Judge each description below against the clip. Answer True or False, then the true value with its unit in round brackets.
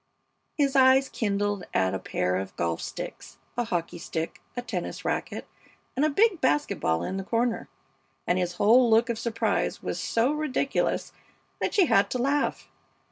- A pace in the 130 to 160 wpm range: False (170 wpm)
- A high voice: True (230 Hz)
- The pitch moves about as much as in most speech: False (6.8 semitones)